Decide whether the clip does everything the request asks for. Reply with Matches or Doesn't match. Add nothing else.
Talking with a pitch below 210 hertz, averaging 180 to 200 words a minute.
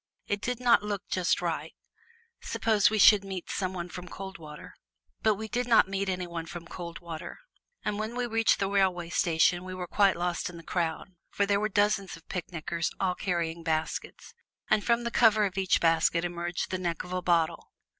Matches